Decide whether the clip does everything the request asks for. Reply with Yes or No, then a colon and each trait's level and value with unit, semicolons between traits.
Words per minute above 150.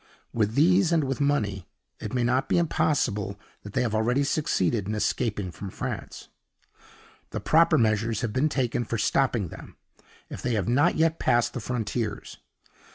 Yes: average, 165 wpm